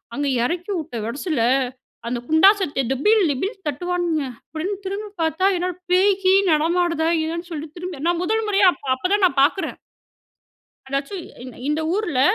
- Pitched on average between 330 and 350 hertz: Yes, very high, 340 Hz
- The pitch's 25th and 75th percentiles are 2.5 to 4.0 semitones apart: No, average, 4.4 semitones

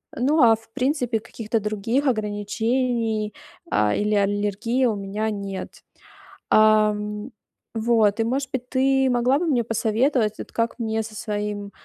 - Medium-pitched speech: No, high, 220 Hz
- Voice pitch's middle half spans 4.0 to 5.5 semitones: No, average, 2.9 semitones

